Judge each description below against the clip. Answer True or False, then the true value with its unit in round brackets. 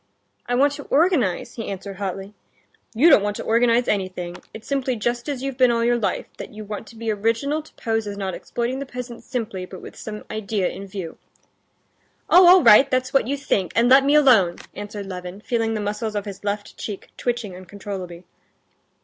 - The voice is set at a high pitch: True (220 Hz)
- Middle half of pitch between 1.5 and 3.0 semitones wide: False (4.0 semitones)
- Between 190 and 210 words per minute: True (200 wpm)